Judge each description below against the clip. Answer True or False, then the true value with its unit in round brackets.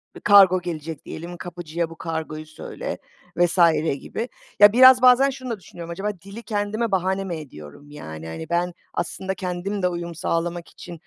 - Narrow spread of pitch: False (3.5 semitones)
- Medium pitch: True (175 Hz)